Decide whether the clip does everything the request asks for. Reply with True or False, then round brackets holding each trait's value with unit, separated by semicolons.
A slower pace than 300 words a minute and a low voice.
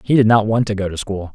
False (355 wpm; 105 Hz)